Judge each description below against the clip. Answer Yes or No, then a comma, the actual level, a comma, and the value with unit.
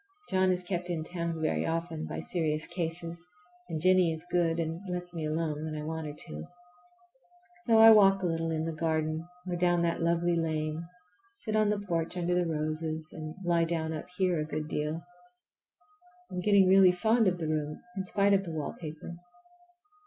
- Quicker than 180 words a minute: Yes, average, 190 wpm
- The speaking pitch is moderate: Yes, medium, 165 Hz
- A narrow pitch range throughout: Yes, narrow, 2.3 semitones